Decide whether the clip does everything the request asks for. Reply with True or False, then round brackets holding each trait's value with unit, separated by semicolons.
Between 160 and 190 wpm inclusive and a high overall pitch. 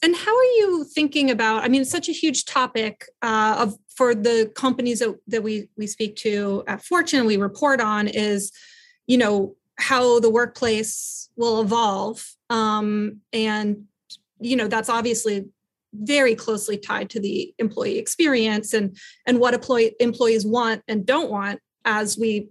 True (165 wpm; 225 Hz)